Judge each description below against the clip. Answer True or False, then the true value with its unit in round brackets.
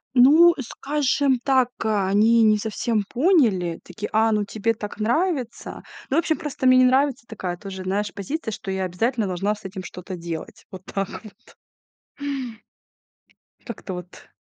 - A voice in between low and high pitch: False (220 Hz)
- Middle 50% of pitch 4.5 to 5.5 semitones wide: True (5.0 semitones)